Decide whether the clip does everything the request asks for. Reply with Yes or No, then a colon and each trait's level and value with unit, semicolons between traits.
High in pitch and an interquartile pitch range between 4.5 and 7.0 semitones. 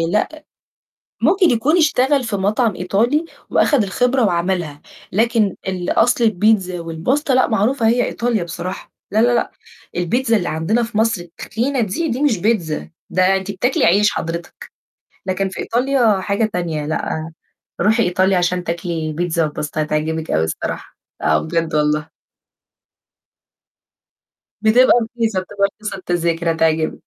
Yes: high, 195 Hz; wide, 5.5 semitones